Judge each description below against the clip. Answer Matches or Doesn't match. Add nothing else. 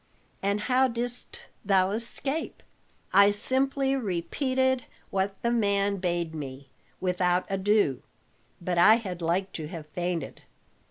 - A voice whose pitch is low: Doesn't match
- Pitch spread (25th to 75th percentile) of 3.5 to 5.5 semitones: Matches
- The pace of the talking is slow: Matches